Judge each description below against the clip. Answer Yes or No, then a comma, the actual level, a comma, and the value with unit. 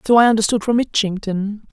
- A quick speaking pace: No, average, 175 wpm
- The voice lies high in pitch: Yes, high, 215 Hz